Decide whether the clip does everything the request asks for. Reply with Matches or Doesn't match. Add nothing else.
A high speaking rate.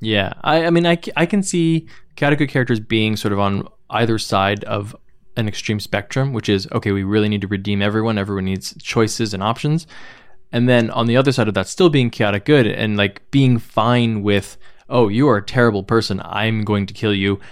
Matches